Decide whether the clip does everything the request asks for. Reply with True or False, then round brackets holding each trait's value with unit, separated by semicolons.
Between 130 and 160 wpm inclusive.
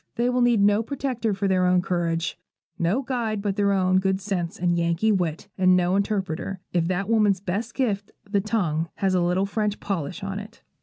False (200 wpm)